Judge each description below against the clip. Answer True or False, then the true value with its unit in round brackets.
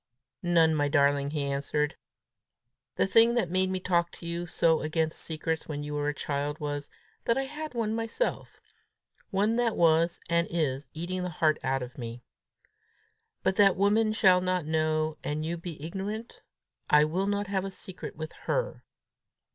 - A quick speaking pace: False (170 wpm)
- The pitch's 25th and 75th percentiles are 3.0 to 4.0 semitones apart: False (4.5 semitones)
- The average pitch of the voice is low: False (170 Hz)